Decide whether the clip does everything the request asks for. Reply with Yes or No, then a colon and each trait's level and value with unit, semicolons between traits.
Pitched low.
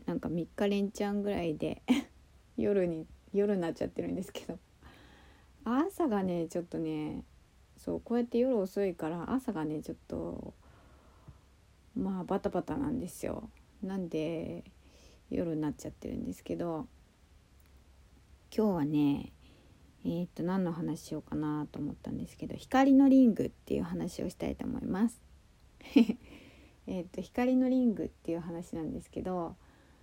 No: medium, 175 Hz